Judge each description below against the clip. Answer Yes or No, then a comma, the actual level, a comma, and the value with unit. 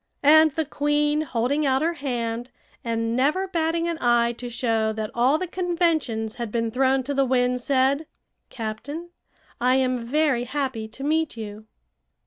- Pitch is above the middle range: Yes, very high, 260 Hz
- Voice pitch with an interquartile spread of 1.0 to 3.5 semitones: No, average, 4.5 semitones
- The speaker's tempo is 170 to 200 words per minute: No, average, 160 wpm